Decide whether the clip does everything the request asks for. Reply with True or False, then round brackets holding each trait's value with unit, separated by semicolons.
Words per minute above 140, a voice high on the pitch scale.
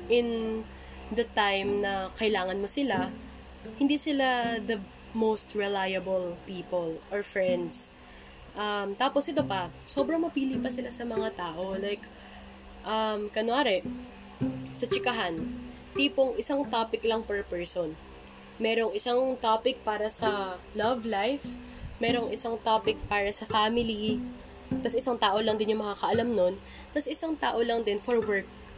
False (135 wpm; 220 Hz)